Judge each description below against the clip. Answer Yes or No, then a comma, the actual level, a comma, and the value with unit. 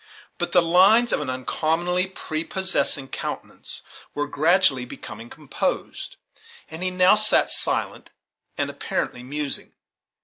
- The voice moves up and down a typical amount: Yes, average, 4.6 semitones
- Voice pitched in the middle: Yes, medium, 165 Hz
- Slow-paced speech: Yes, slow, 115 wpm